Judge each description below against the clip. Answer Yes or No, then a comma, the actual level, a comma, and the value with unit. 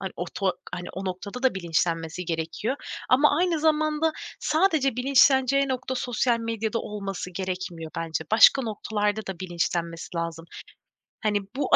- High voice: Yes, high, 210 Hz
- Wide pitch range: Yes, wide, 6.9 semitones